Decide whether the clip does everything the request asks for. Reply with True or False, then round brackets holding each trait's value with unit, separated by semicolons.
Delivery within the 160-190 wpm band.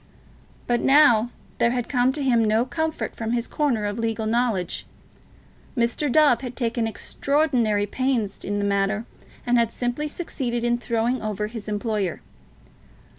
False (150 wpm)